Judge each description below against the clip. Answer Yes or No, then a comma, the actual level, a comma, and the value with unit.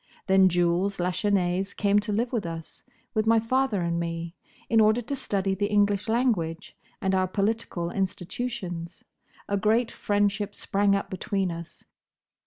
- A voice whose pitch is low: No, high, 200 Hz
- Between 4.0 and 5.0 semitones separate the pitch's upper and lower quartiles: No, average, 3.4 semitones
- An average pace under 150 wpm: Yes, average, 140 wpm